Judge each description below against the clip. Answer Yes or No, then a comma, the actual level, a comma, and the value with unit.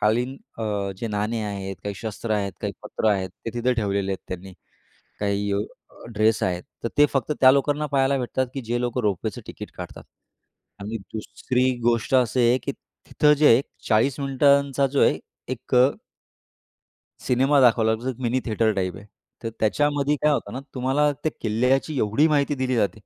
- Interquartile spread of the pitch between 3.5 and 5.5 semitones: Yes, average, 4.1 semitones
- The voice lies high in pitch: No, low, 120 Hz